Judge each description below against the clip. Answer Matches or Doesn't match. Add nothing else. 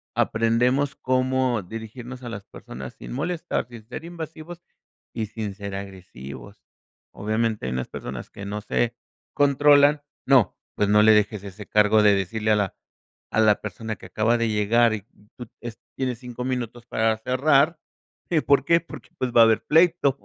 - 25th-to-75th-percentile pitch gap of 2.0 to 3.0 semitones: Doesn't match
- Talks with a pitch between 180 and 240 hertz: Doesn't match